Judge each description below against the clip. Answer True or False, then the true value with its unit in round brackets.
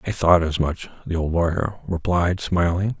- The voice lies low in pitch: True (85 Hz)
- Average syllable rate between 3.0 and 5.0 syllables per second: True (4.6 syllables/s)